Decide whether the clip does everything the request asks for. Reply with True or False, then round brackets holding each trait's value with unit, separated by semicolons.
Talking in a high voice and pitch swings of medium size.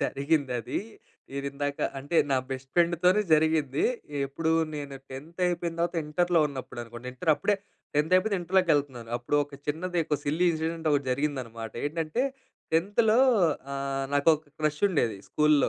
False (150 Hz; 3.5 semitones)